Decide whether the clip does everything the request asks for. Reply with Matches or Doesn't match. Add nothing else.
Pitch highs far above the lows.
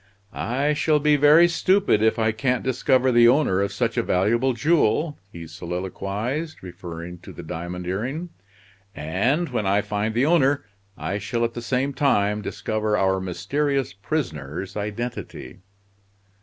Matches